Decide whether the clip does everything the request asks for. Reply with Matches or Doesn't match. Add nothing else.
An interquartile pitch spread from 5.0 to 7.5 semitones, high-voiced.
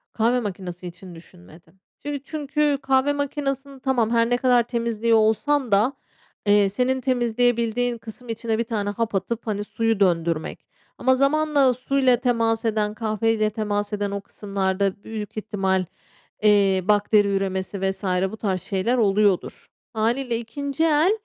Doesn't match